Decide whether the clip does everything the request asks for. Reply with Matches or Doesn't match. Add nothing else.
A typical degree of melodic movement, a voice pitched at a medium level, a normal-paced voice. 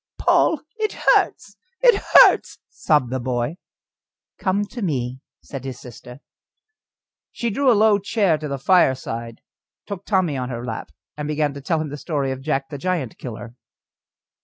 Doesn't match